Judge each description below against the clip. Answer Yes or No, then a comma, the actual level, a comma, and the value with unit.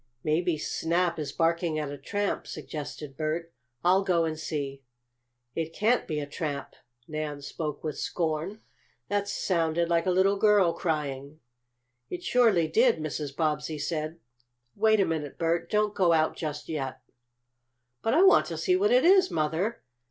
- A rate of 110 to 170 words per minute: Yes, average, 160 wpm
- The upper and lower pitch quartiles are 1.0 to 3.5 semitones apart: No, average, 4.1 semitones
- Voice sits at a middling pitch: Yes, medium, 165 Hz